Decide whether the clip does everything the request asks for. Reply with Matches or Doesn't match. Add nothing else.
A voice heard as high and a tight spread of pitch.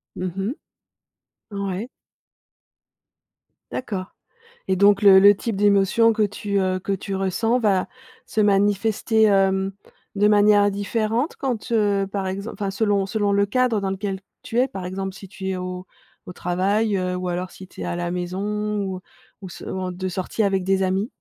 Matches